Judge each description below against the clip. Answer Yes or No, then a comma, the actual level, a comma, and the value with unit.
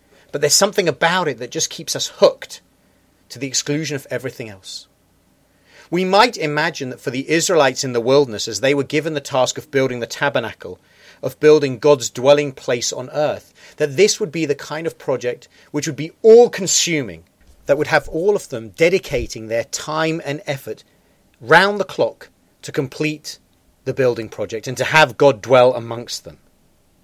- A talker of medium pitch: Yes, medium, 145 Hz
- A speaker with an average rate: Yes, average, 180 wpm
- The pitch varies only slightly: No, average, 4.3 semitones